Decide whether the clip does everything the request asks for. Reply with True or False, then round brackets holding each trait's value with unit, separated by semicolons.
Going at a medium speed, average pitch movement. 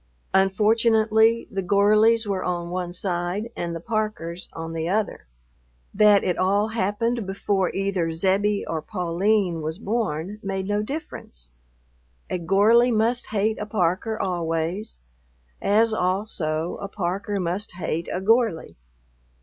False (130 wpm; 3.6 semitones)